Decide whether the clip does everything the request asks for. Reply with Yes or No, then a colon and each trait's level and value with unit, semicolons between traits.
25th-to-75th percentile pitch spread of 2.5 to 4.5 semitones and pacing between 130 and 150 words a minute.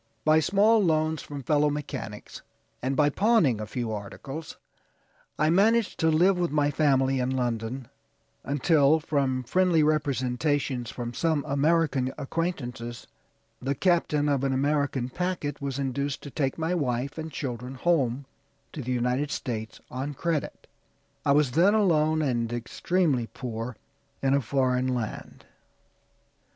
Yes: average, 3.7 semitones; average, 140 wpm